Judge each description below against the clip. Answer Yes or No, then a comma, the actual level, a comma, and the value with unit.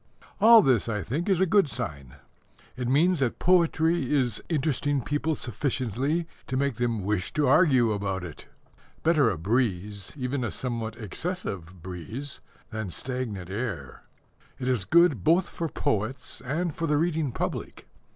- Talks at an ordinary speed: Yes, average, 150 wpm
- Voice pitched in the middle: No, low, 130 Hz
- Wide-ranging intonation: Yes, wide, 6.7 semitones